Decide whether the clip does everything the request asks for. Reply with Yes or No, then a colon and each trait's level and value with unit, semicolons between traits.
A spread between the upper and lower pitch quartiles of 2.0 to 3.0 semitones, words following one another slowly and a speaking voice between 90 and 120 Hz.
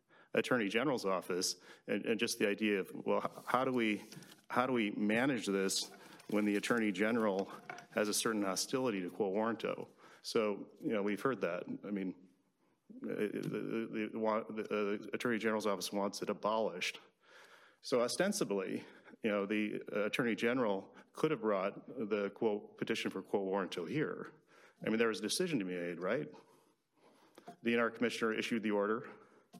No: narrow, 2.4 semitones; average, 170 wpm; low, 105 Hz